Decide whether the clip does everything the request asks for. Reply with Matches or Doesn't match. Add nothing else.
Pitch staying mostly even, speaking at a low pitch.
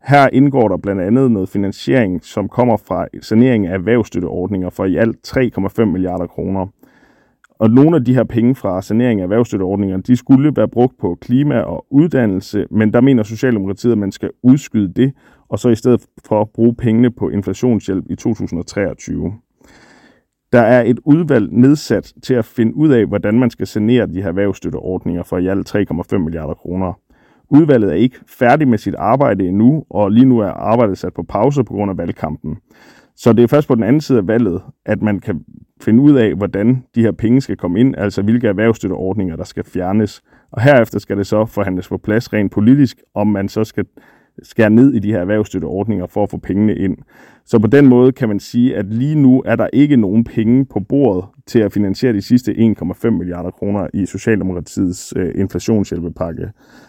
Doesn't match